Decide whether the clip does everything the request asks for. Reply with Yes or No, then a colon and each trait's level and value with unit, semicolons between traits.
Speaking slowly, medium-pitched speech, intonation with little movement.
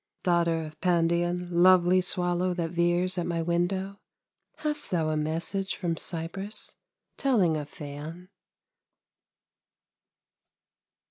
Yes: slow, 105 wpm; medium, 175 Hz; narrow, 1.8 semitones